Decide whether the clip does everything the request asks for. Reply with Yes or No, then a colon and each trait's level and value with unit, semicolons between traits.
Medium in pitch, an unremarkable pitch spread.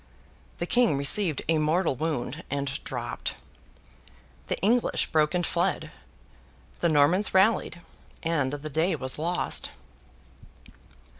Yes: medium, 160 Hz; average, 4.1 semitones